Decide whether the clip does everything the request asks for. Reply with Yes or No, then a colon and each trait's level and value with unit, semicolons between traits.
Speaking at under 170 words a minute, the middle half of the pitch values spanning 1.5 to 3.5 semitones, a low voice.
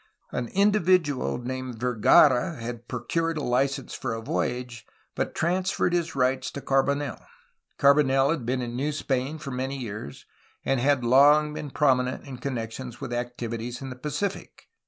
Yes: average, 155 wpm; average, 3.1 semitones; low, 130 Hz